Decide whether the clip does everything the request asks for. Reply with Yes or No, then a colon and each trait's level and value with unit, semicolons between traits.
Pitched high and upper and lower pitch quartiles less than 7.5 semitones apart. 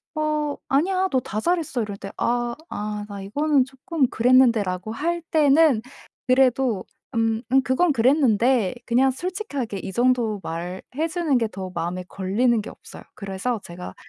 Yes: high, 245 Hz; wide, 5.4 semitones